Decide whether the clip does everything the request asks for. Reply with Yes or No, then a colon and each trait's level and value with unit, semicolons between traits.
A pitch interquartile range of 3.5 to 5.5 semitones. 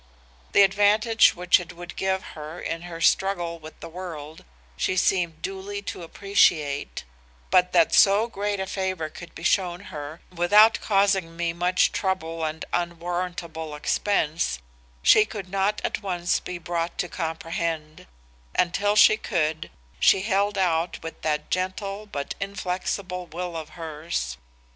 No: average, 3.0 semitones